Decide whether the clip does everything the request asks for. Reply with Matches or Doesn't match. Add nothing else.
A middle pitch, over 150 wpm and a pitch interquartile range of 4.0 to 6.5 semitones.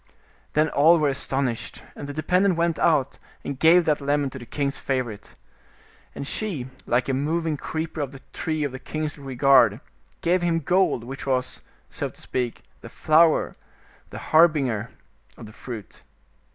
Doesn't match